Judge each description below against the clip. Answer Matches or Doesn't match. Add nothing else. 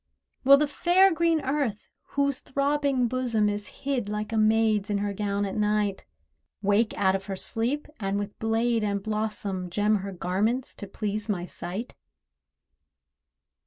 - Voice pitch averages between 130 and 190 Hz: Doesn't match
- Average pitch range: Matches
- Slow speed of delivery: Doesn't match